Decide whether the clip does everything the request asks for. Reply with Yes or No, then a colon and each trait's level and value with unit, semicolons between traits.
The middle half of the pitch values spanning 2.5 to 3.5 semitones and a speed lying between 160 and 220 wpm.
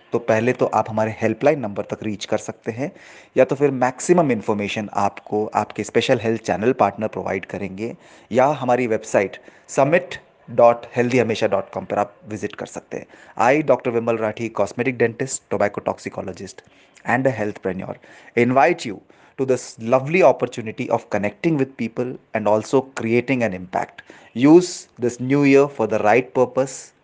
Yes: average, 3.2 semitones; average, 165 wpm